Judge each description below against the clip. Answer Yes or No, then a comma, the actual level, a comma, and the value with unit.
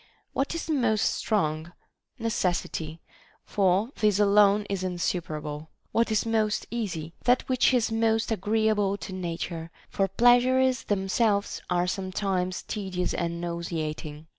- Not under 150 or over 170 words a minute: No, average, 140 wpm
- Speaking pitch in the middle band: No, high, 200 Hz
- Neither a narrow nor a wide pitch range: Yes, average, 4.3 semitones